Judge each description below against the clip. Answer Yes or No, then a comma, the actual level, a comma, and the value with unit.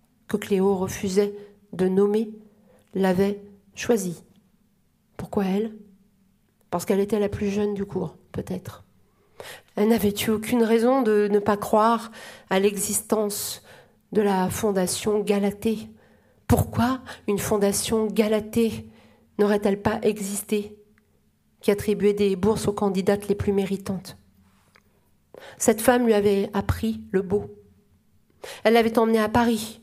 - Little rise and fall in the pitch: Yes, narrow, 2.0 semitones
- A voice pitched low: No, high, 205 Hz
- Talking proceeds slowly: Yes, slow, 125 wpm